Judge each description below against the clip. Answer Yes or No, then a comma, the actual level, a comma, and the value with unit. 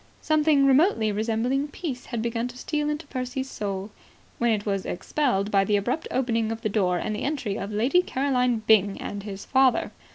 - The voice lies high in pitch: Yes, high, 235 Hz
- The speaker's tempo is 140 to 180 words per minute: No, average, 190 wpm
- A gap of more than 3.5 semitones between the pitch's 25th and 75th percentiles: Yes, average, 4.6 semitones